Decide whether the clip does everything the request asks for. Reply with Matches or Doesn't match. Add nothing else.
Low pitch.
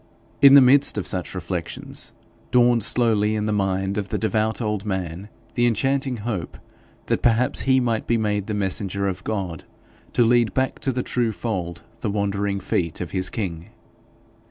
Matches